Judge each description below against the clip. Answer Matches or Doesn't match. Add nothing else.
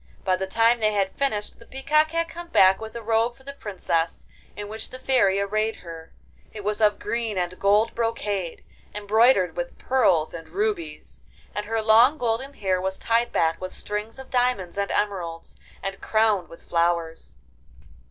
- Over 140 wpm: Matches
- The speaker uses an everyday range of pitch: Matches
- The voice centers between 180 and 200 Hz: Doesn't match